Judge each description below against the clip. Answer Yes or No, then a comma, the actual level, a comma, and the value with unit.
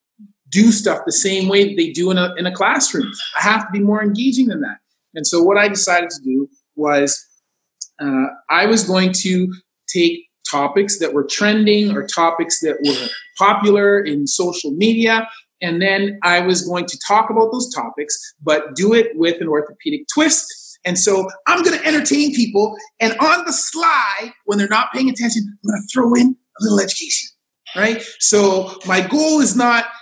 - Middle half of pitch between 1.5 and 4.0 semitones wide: No, average, 5.0 semitones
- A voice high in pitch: Yes, high, 205 Hz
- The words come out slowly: No, average, 190 wpm